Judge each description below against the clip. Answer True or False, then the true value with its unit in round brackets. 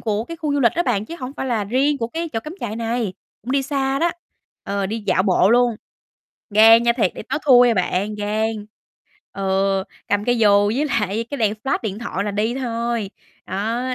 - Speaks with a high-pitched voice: True (225 Hz)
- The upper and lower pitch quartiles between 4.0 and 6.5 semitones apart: False (3.5 semitones)